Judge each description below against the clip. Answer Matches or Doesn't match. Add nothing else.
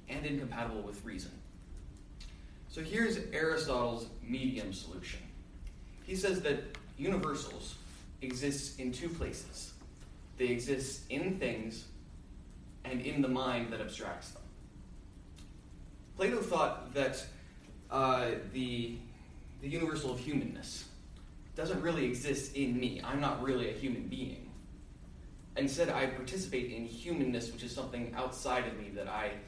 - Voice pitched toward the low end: Matches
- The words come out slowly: Matches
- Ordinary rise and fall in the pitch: Doesn't match